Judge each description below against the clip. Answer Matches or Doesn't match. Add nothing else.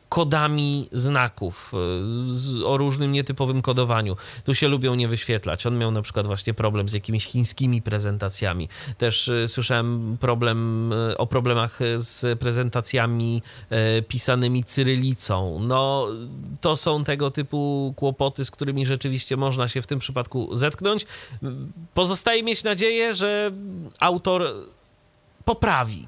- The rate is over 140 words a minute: Doesn't match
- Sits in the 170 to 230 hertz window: Doesn't match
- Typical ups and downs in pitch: Matches